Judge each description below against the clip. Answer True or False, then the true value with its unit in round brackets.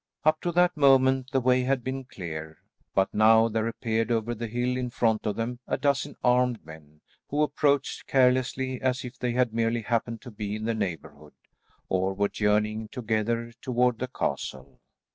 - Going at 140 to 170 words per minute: False (180 wpm)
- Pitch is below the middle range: True (120 Hz)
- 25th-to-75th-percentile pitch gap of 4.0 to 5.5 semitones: False (3.1 semitones)